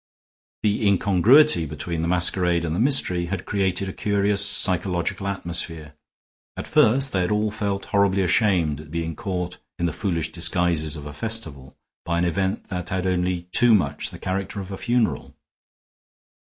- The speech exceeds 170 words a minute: No, average, 165 wpm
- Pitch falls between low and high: No, very low, 90 Hz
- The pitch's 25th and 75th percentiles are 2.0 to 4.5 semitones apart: Yes, average, 3.0 semitones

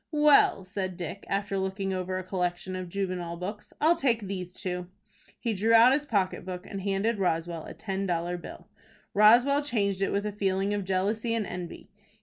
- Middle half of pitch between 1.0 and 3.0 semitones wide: Yes, narrow, 2.5 semitones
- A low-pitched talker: No, high, 195 Hz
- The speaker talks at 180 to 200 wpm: Yes, average, 185 wpm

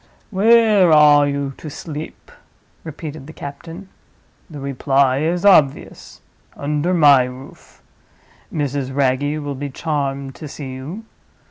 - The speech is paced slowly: Yes, slow, 115 wpm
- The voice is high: No, medium, 145 Hz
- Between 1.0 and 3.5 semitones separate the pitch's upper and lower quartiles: Yes, average, 2.7 semitones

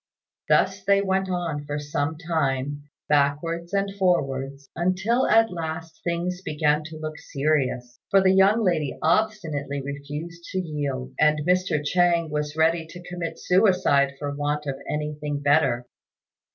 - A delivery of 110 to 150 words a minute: Yes, average, 140 wpm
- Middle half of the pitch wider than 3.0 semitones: Yes, average, 3.8 semitones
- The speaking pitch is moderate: Yes, medium, 155 Hz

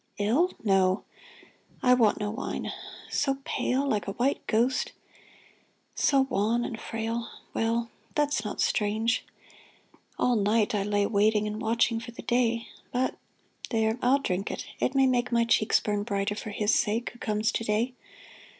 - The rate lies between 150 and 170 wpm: Yes, average, 160 wpm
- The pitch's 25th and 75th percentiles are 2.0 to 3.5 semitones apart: Yes, narrow, 2.5 semitones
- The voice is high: Yes, high, 225 Hz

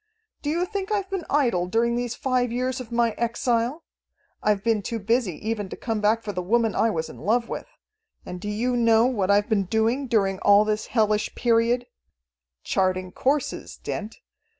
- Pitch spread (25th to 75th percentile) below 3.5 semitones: Yes, average, 2.9 semitones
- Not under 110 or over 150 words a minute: No, average, 185 wpm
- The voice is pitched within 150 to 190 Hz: No, high, 230 Hz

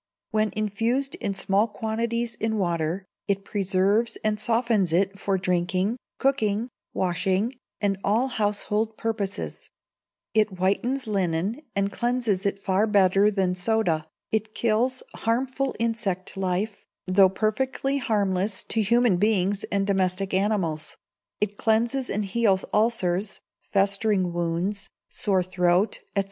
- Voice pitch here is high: Yes, high, 205 Hz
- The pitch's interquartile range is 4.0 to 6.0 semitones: No, average, 2.9 semitones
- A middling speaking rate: No, slow, 125 wpm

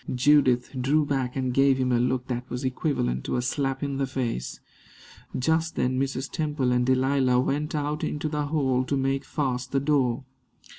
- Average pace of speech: Yes, average, 185 wpm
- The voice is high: No, low, 135 Hz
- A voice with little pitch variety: Yes, narrow, 2.3 semitones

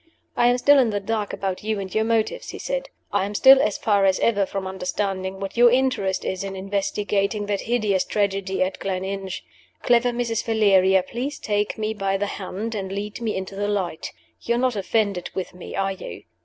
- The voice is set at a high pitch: Yes, high, 205 Hz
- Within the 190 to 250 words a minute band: Yes, average, 200 wpm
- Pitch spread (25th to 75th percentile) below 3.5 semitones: Yes, average, 2.9 semitones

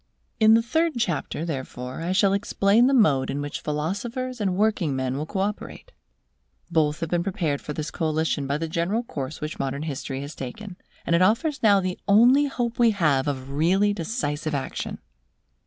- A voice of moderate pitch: Yes, medium, 170 Hz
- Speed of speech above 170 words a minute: Yes, average, 185 wpm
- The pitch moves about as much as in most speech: No, wide, 6.5 semitones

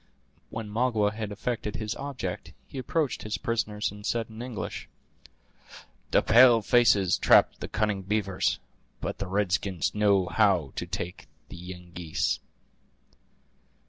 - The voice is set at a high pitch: No, low, 105 Hz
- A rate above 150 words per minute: No, slow, 135 wpm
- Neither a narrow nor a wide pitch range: Yes, average, 3.1 semitones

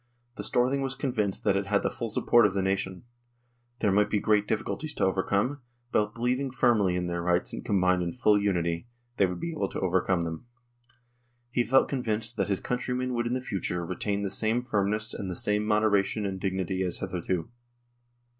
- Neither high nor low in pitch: No, low, 105 Hz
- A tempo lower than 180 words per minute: No, average, 200 wpm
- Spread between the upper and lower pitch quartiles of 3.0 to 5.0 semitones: Yes, average, 4.0 semitones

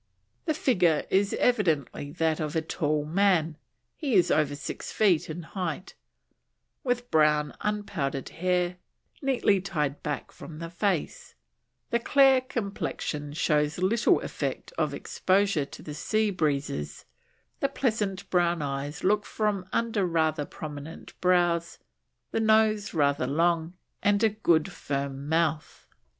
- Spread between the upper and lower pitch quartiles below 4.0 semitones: No, average, 5.3 semitones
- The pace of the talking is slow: Yes, slow, 130 wpm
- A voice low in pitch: No, medium, 175 Hz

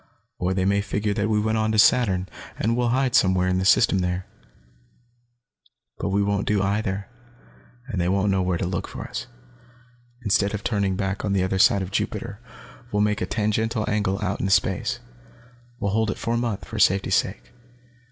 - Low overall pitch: Yes, low, 100 Hz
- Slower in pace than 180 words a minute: No, average, 195 wpm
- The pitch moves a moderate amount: No, narrow, 2.2 semitones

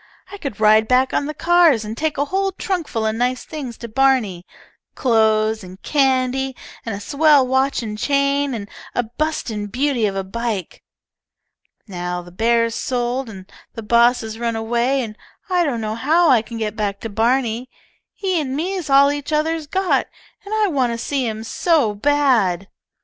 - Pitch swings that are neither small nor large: Yes, average, 4.7 semitones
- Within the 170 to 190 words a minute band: Yes, average, 180 wpm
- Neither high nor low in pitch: No, high, 245 Hz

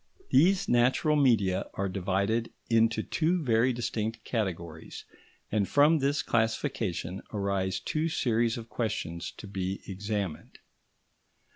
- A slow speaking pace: Yes, slow, 115 wpm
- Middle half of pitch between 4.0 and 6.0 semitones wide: Yes, average, 4.3 semitones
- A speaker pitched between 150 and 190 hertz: No, low, 110 Hz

